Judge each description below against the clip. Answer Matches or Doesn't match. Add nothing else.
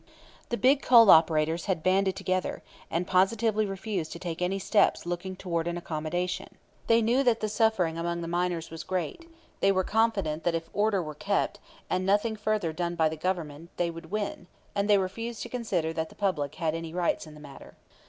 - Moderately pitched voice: Matches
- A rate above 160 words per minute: Matches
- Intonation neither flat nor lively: Matches